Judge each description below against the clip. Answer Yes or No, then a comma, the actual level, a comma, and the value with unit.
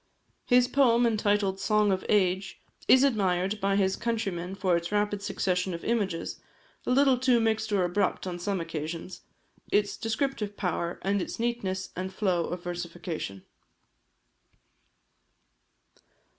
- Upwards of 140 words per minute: No, slow, 135 wpm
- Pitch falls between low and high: No, high, 195 Hz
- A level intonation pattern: No, average, 3.5 semitones